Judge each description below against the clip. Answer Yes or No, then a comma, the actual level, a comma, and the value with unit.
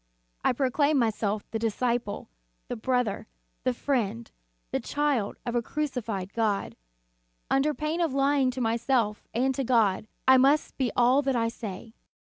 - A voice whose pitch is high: Yes, high, 245 Hz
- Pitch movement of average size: Yes, average, 3.6 semitones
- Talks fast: No, average, 155 wpm